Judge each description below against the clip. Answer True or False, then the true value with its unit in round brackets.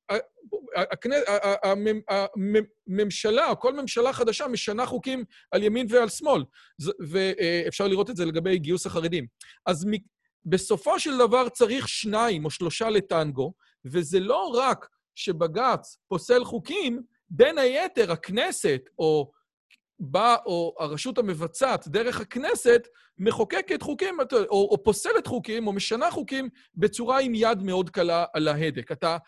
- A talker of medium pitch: False (215 Hz)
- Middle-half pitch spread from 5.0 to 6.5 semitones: True (5.6 semitones)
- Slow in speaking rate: False (125 wpm)